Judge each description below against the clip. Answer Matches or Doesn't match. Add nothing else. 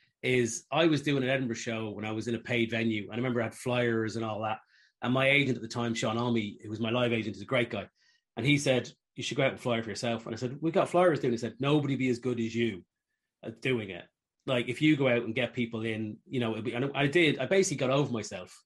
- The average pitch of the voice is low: Matches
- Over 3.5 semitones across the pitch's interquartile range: Doesn't match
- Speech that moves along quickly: Matches